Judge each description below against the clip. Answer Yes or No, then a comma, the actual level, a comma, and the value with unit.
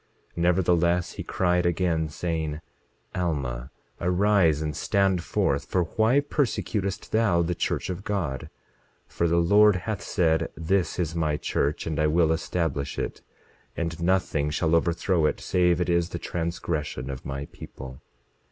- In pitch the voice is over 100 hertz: No, very low, 85 Hz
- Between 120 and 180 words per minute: Yes, average, 150 wpm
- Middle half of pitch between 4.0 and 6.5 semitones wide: No, narrow, 2.6 semitones